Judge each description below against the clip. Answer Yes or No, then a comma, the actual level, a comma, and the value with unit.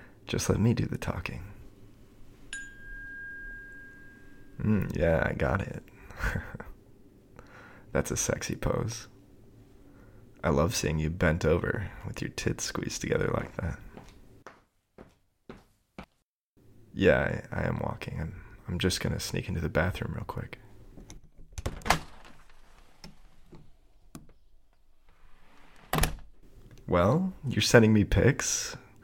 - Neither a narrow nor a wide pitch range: Yes, average, 5.0 semitones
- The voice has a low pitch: Yes, low, 105 Hz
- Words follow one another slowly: Yes, slow, 100 wpm